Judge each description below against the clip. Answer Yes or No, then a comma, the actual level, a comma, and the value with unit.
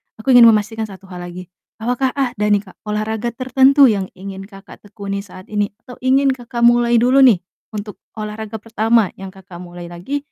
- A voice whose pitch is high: Yes, high, 215 Hz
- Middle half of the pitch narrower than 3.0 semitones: No, average, 3.7 semitones